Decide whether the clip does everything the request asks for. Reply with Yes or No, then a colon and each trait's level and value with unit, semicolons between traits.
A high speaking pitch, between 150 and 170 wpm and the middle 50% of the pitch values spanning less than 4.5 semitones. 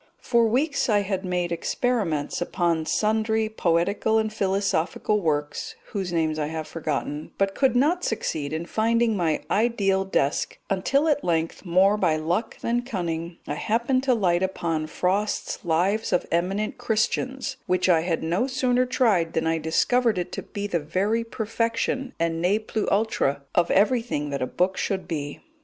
No: high, 195 Hz; average, 160 wpm; wide, 5.4 semitones